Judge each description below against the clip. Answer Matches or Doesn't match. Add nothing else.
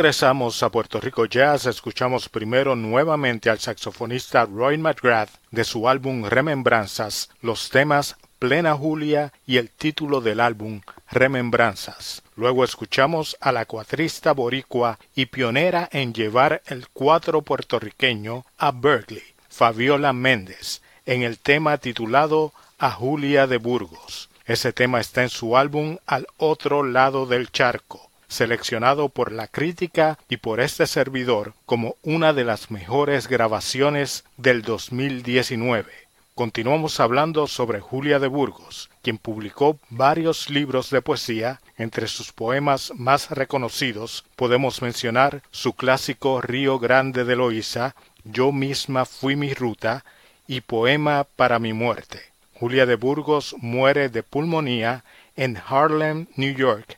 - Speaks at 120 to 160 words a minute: Matches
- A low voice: Matches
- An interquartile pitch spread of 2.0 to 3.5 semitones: Matches